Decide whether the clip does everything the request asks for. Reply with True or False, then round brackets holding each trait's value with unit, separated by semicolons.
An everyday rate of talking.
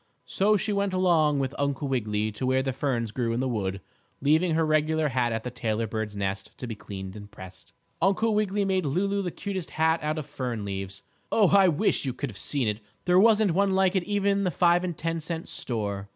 False (225 wpm)